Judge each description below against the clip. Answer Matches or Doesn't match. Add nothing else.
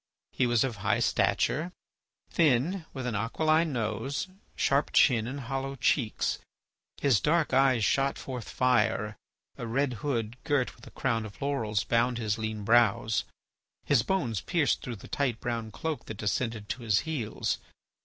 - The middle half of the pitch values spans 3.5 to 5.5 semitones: Matches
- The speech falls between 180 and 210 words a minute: Doesn't match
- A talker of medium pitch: Doesn't match